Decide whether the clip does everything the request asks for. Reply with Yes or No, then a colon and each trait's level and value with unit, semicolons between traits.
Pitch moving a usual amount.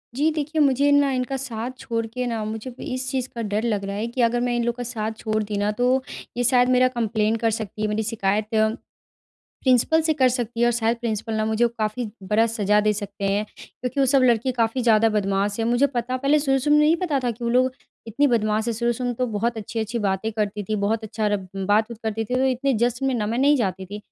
Yes: average, 3.0 semitones